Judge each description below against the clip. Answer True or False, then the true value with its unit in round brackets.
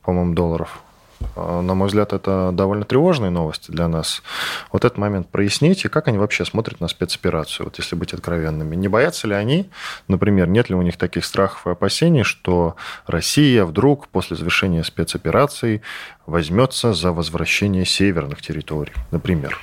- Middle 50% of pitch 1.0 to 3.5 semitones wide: False (3.9 semitones)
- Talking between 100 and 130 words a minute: False (155 wpm)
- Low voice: True (95 Hz)